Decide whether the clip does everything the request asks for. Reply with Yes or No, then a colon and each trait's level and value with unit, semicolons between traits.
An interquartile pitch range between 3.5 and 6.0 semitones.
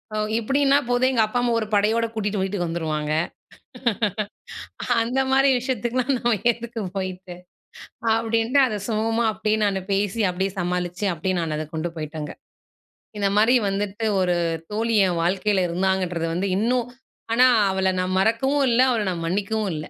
Yes: average, 4.2 semitones